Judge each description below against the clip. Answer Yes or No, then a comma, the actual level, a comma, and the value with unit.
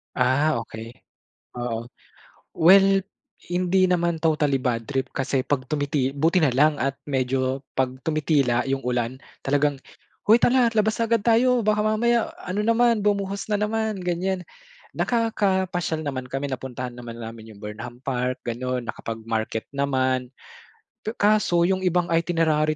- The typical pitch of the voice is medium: Yes, medium, 150 Hz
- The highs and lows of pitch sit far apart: Yes, wide, 7.1 semitones